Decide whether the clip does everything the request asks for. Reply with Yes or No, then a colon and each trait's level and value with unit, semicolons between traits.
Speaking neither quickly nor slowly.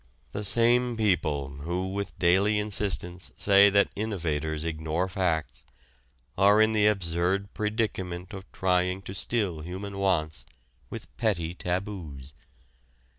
No: slow, 120 wpm